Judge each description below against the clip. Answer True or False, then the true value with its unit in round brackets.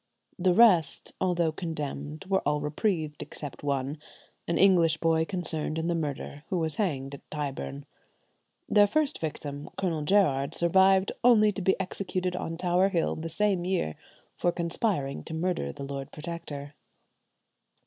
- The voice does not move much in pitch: False (4.2 semitones)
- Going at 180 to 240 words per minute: False (150 wpm)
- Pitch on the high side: False (165 Hz)